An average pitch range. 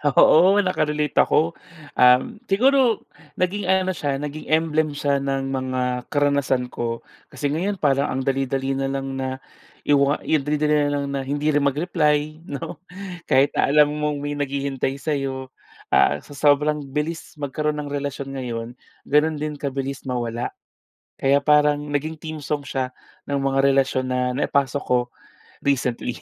No: narrow, 2.0 semitones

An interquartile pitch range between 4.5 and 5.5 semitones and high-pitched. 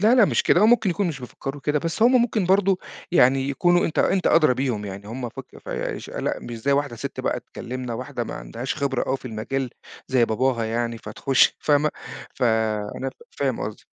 No: average, 4.8 semitones; low, 135 Hz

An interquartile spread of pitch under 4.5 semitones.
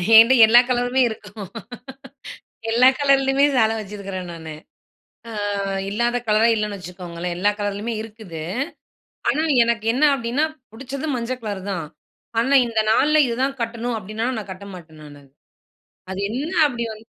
Yes: average, 3.8 semitones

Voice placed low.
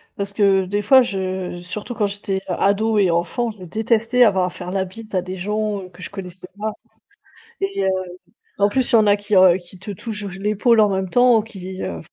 No: high, 200 Hz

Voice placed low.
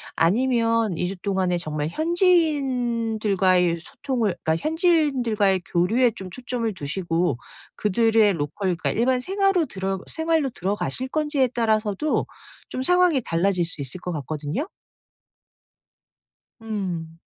No: high, 215 Hz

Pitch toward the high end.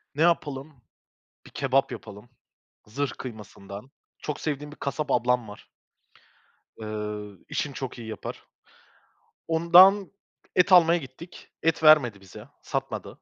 No: low, 135 Hz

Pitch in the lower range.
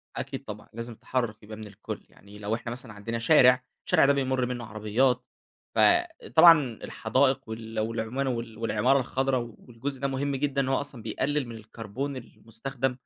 Yes: low, 125 Hz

